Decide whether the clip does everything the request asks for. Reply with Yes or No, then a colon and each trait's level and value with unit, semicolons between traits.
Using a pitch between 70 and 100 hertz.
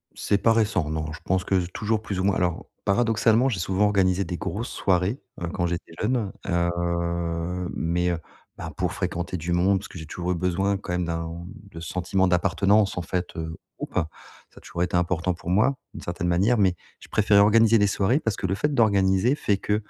Yes: very low, 95 Hz